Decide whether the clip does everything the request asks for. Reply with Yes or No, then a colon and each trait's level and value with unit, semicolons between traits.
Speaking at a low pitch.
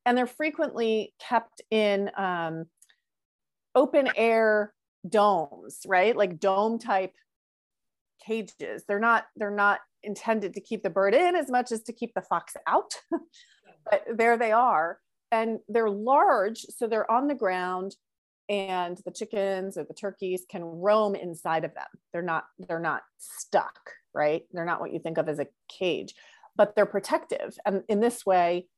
No: high, 205 Hz